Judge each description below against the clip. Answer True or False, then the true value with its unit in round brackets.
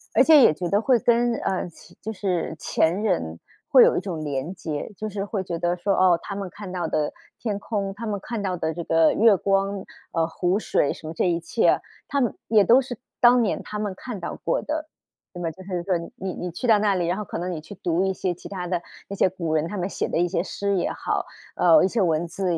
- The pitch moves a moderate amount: True (3.4 semitones)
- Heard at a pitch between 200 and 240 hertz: False (185 Hz)